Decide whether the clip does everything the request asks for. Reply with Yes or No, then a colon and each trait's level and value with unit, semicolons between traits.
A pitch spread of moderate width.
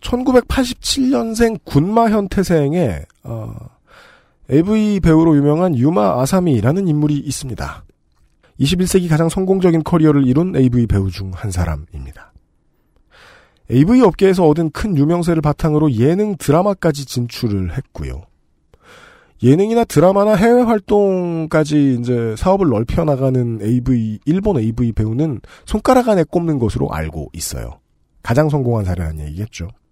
No: wide, 8.3 semitones